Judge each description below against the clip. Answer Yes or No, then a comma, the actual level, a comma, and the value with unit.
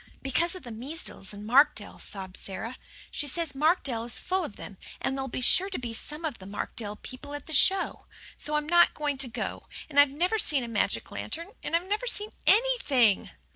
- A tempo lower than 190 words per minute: No, average, 200 wpm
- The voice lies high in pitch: Yes, very high, 285 Hz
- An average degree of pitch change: No, wide, 6.3 semitones